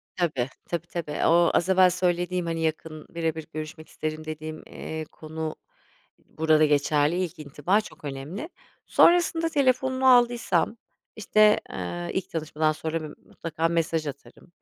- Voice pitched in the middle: Yes, medium, 160 Hz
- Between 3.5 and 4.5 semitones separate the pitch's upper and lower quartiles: No, average, 2.9 semitones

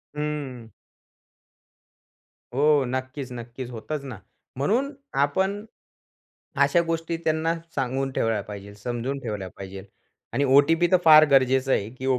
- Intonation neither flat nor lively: Yes, average, 4.2 semitones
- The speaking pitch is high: No, low, 135 Hz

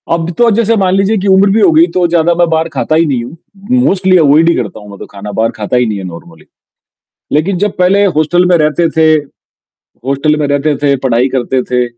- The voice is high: No, medium, 160 Hz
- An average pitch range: No, wide, 6.2 semitones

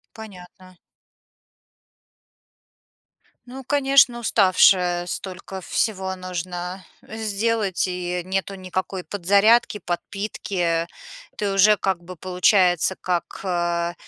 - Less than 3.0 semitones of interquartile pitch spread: Yes, narrow, 2.5 semitones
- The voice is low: No, medium, 185 Hz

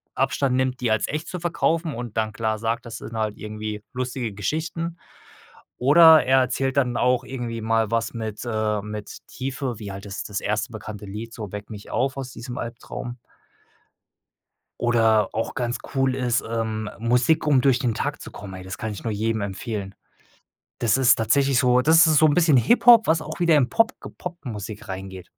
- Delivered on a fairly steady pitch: No, average, 3.7 semitones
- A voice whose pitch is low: Yes, low, 120 Hz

